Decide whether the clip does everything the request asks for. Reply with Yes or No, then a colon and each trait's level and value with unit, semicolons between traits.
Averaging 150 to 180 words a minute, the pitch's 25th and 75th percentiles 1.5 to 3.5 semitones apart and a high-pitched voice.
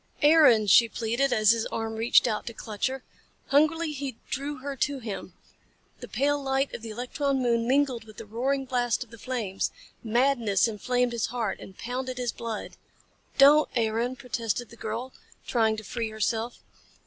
Yes: average, 170 wpm; average, 3.2 semitones; high, 240 Hz